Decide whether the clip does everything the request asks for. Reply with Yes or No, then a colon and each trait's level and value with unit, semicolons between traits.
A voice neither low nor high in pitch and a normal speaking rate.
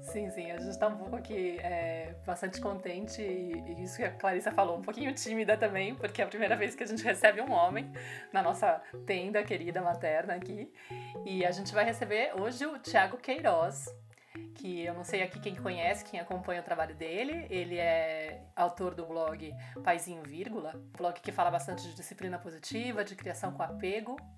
No: medium, 180 Hz; fast, 190 wpm